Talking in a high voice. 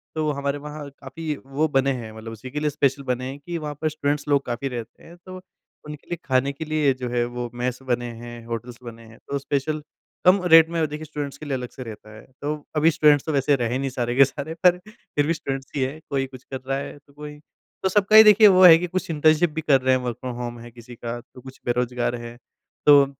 No: medium, 140 Hz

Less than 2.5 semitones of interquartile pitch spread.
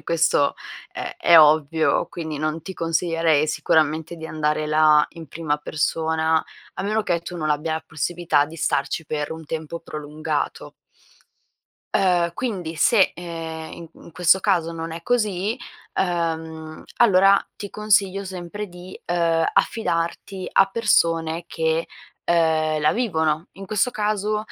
No: average, 2.8 semitones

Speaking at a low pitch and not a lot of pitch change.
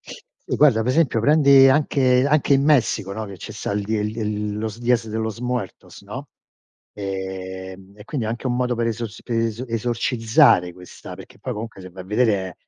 No: low, 110 Hz; average, 3.8 semitones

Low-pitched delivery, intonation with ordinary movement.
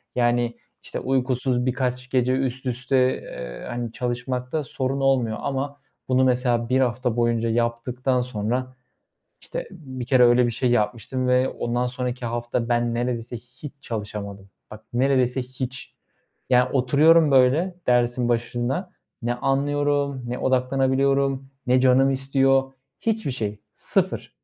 No: low, 125 Hz; narrow, 1.9 semitones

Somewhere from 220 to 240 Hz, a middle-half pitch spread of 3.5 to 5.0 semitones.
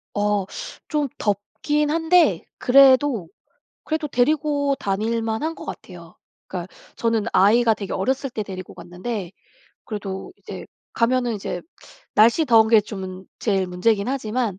No: high, 225 Hz; wide, 5.5 semitones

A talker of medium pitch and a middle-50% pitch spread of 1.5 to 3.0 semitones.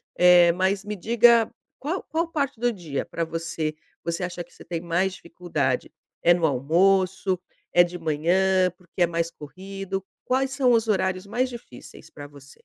No: medium, 180 Hz; average, 3.5 semitones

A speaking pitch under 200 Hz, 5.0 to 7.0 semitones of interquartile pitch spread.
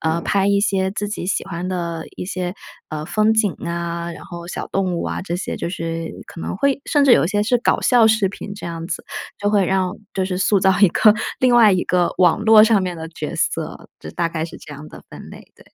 No: medium, 185 Hz; average, 3.5 semitones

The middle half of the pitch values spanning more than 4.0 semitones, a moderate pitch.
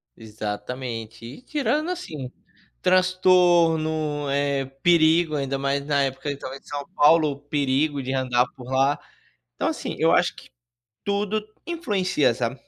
Yes: average, 4.6 semitones; medium, 145 Hz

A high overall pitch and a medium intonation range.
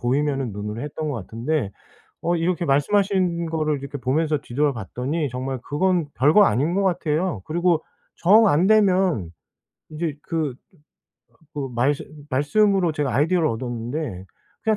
No: medium, 150 Hz; average, 4.9 semitones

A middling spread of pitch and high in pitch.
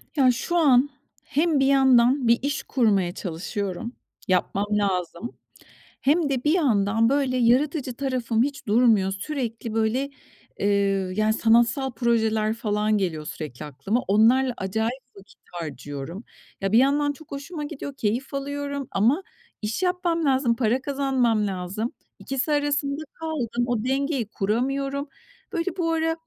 Yes: average, 4.8 semitones; high, 245 Hz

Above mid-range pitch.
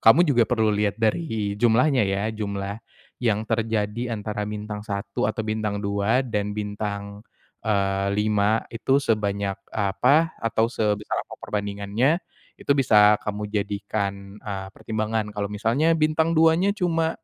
No: low, 105 Hz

